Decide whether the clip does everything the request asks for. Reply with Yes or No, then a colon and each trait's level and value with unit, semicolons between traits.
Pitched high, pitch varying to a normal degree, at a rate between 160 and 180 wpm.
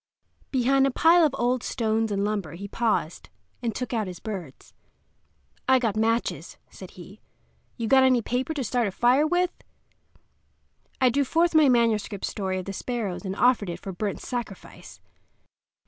Yes: high, 230 Hz; average, 4.3 semitones; average, 165 wpm